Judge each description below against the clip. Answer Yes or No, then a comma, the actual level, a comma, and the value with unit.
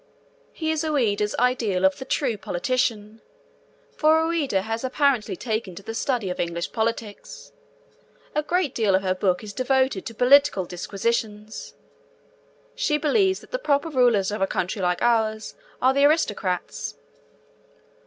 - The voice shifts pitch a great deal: Yes, wide, 5.9 semitones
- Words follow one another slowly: No, average, 145 wpm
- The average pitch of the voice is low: No, high, 230 Hz